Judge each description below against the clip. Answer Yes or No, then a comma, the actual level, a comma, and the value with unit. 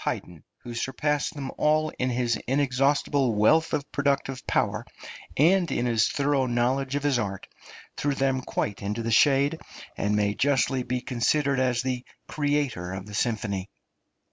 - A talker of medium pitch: No, low, 130 Hz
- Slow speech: No, average, 155 wpm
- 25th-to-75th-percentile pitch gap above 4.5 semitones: No, average, 3.5 semitones